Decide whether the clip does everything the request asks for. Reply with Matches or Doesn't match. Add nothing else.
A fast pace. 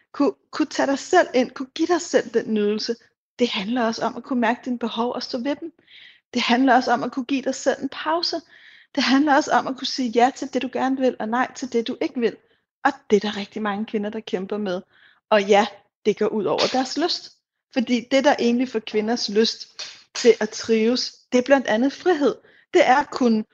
Matches